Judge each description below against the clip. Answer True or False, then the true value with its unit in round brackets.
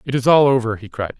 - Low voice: True (125 Hz)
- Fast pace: True (305 wpm)